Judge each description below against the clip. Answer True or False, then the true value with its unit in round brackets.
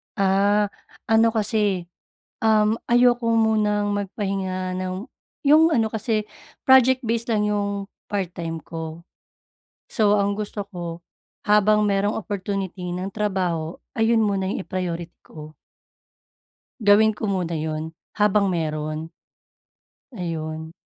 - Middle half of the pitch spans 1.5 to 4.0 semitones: True (3.3 semitones)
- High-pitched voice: True (200 Hz)